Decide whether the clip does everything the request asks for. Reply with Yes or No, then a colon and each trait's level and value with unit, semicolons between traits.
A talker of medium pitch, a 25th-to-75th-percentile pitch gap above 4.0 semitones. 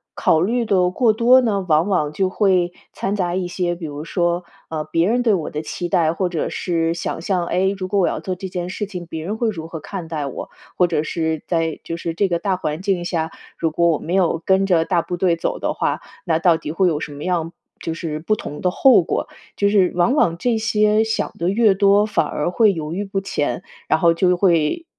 No: medium, 180 Hz; average, 3.2 semitones